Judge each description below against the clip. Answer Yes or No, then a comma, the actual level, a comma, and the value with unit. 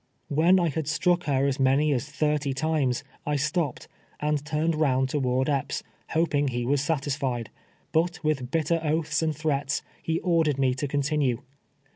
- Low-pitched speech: No, medium, 150 Hz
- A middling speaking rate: Yes, average, 160 wpm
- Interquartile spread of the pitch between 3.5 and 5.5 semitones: No, average, 2.8 semitones